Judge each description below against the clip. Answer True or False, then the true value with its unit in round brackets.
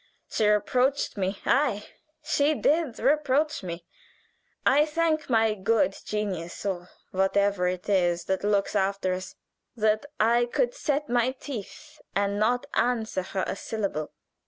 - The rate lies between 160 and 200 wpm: False (135 wpm)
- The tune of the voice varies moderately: False (5.9 semitones)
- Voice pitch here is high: True (215 Hz)